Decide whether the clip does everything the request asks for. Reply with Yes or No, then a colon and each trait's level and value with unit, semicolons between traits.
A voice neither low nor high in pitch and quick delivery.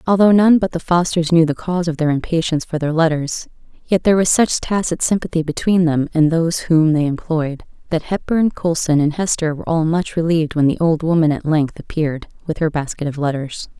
Yes: medium, 165 Hz; fast, 210 wpm